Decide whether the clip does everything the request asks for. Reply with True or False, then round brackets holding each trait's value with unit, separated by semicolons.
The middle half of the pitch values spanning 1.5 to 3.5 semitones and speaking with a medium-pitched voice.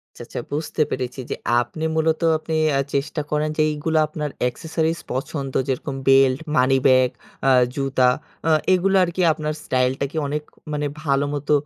True (2.8 semitones; 145 Hz)